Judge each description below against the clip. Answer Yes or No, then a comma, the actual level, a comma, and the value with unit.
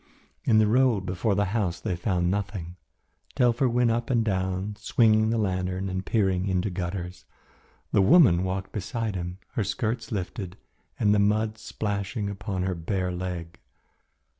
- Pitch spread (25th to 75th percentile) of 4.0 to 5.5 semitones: No, average, 3.1 semitones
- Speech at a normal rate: Yes, average, 155 wpm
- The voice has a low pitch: Yes, low, 100 Hz